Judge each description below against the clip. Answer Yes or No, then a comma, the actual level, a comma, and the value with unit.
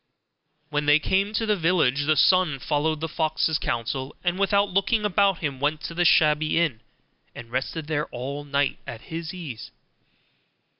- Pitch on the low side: No, medium, 155 Hz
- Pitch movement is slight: No, average, 4.0 semitones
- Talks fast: No, average, 165 wpm